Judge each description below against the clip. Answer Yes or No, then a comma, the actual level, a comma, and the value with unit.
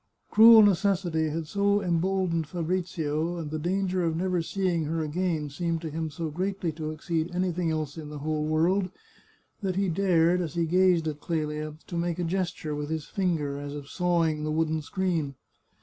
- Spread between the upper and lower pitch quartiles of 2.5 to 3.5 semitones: Yes, average, 2.9 semitones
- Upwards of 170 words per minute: Yes, average, 185 wpm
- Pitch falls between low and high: Yes, medium, 165 Hz